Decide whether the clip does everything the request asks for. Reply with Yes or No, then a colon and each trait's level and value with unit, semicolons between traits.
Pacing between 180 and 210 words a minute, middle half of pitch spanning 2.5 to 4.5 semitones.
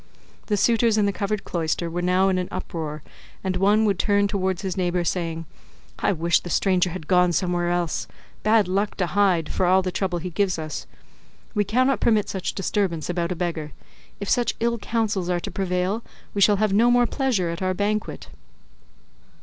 Yes: average, 190 wpm; average, 2.9 semitones